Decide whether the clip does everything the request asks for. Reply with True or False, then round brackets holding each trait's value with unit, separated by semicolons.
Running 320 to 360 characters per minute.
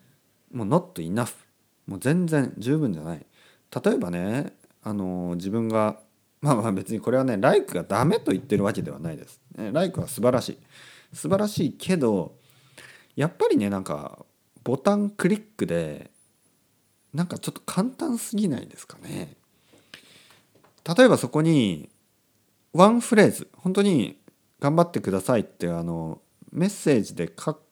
False (305 characters per minute)